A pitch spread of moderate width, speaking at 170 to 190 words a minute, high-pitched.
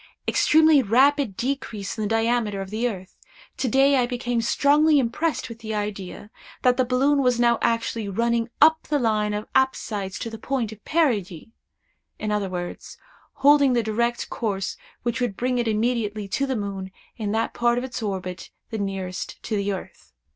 Yes: average, 3.6 semitones; average, 175 wpm; high, 230 Hz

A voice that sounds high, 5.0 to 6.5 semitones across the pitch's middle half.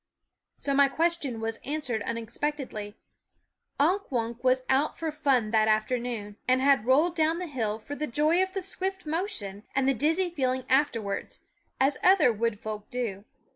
Yes: very high, 265 Hz; wide, 5.5 semitones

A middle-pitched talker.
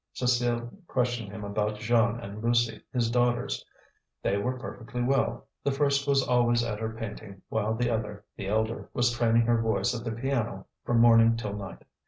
No: low, 115 Hz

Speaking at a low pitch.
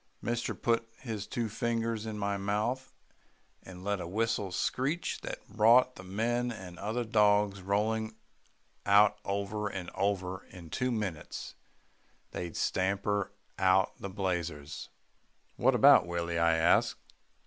Yes: low, 100 Hz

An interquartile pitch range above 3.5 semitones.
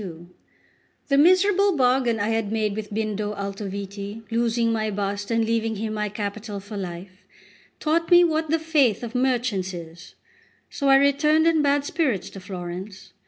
Yes: wide, 5.6 semitones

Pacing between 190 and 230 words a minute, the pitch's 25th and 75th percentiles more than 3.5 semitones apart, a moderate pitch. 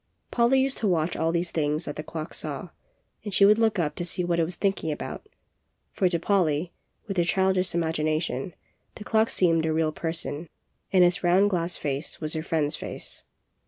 No: average, 195 wpm; average, 3.2 semitones; medium, 170 Hz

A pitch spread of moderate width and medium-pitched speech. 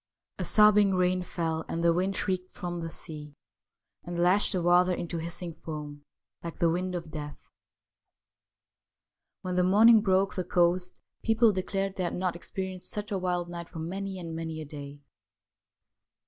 No: narrow, 2.2 semitones; medium, 180 Hz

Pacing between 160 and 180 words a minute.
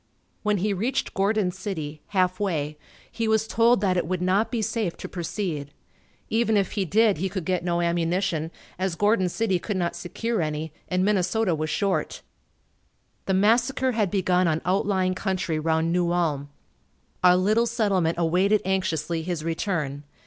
Yes: average, 165 wpm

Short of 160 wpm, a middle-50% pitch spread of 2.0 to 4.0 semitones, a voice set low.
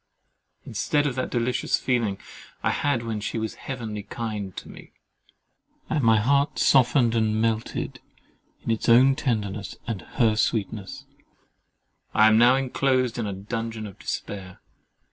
Yes: average, 145 wpm; average, 2.8 semitones; low, 115 Hz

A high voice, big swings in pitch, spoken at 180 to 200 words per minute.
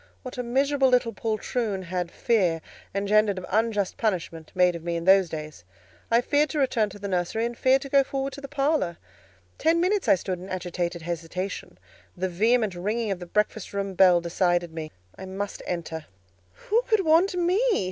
Yes: high, 200 Hz; wide, 6.2 semitones; average, 190 wpm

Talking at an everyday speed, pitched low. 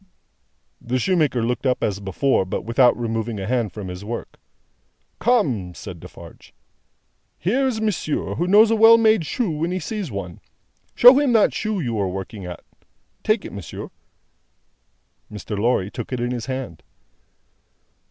Yes: average, 160 wpm; low, 125 Hz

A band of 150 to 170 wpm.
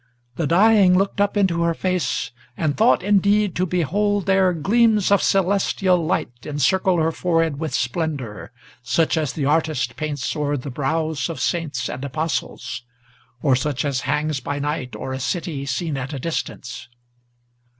Yes: average, 160 wpm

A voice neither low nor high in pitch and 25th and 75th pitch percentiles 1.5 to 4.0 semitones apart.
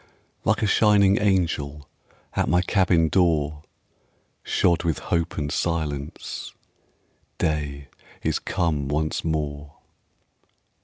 No: very low, 80 Hz; average, 3.3 semitones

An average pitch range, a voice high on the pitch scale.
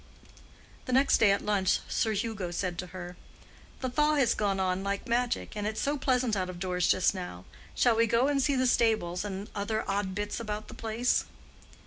Yes: average, 4.2 semitones; high, 210 Hz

